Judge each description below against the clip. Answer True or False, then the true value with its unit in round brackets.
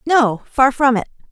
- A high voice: True (255 Hz)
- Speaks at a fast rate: False (185 wpm)